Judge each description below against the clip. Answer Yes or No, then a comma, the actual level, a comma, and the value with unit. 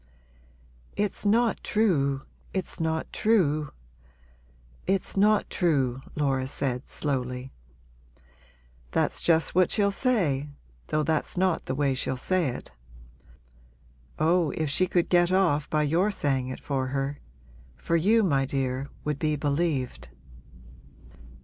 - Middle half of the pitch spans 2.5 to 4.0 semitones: No, average, 5.2 semitones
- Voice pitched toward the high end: No, medium, 150 Hz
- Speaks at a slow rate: Yes, slow, 125 wpm